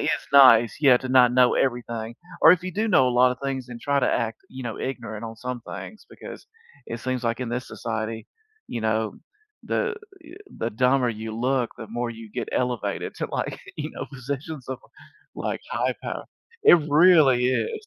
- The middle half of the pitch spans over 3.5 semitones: No, average, 2.8 semitones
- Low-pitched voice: Yes, low, 125 Hz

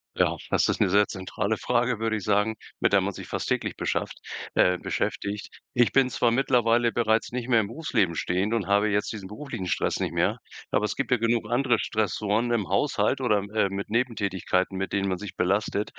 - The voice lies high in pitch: No, low, 105 Hz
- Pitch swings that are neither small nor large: Yes, average, 3.0 semitones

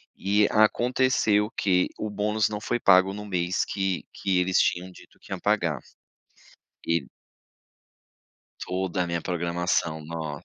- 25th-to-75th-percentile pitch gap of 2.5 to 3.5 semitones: Yes, average, 3.1 semitones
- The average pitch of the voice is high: No, very low, 95 Hz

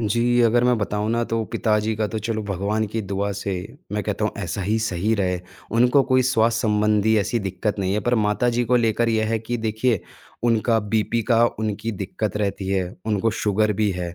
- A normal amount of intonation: No, narrow, 2.1 semitones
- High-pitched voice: No, low, 110 Hz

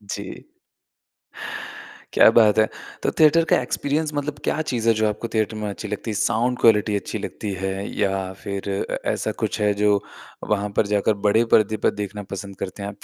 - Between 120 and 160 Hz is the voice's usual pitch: No, low, 105 Hz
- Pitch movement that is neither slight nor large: No, narrow, 2.3 semitones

